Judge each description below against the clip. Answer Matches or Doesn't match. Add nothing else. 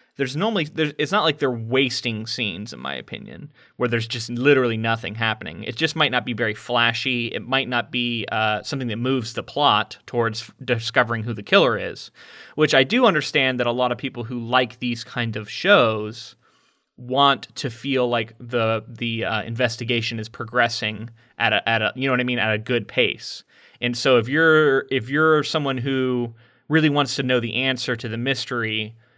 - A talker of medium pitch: Doesn't match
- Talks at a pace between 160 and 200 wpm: Matches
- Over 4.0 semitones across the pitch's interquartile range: Doesn't match